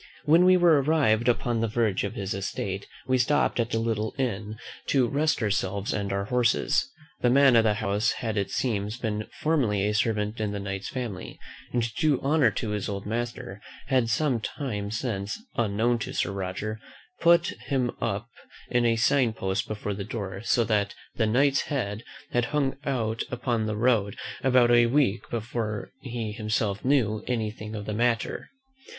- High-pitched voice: No, low, 115 Hz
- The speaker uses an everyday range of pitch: Yes, average, 3.2 semitones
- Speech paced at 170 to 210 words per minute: Yes, average, 180 wpm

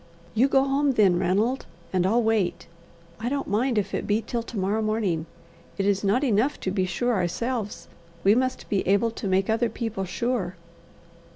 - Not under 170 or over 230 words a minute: Yes, average, 185 wpm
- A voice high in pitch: Yes, high, 215 Hz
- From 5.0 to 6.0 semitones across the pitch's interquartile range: No, average, 3.9 semitones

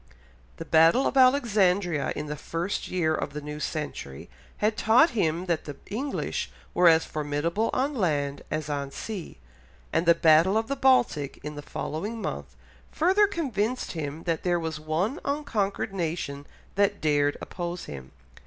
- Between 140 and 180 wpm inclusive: Yes, average, 160 wpm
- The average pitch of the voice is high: No, medium, 170 Hz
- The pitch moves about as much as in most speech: No, wide, 6.4 semitones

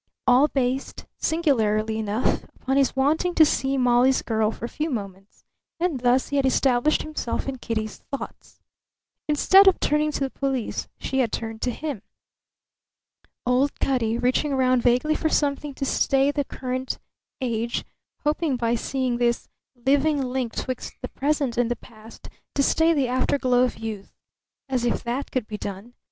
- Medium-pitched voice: No, very high, 255 Hz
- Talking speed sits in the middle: Yes, average, 165 wpm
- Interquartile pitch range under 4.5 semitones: Yes, average, 2.9 semitones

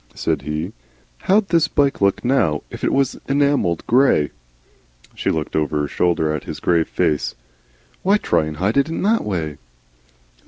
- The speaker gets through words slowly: No, average, 165 wpm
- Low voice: Yes, very low, 95 Hz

